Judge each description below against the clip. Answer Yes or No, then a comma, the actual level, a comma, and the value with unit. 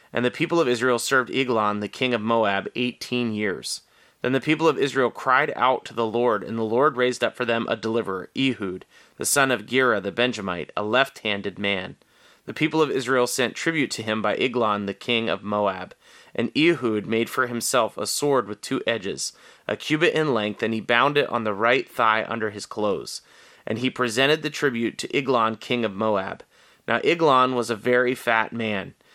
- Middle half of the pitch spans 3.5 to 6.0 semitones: No, average, 2.9 semitones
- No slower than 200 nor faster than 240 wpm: Yes, fast, 205 wpm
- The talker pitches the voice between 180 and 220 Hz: No, low, 120 Hz